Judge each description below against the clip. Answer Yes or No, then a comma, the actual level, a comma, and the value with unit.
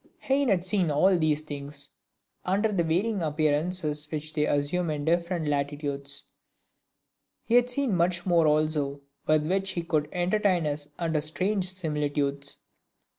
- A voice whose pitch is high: No, medium, 160 Hz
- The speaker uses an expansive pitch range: No, average, 3.7 semitones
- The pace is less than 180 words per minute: Yes, average, 140 wpm